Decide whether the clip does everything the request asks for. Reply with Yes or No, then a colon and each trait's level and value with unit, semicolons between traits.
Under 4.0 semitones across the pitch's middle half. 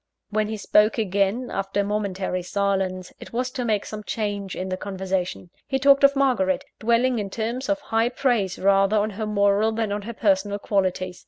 Yes: average, 2.9 semitones